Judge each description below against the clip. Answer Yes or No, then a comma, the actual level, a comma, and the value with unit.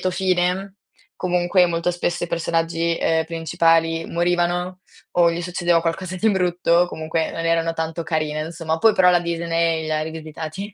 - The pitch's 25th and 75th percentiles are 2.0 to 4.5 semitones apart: No, narrow, 1.4 semitones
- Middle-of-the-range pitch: Yes, medium, 170 Hz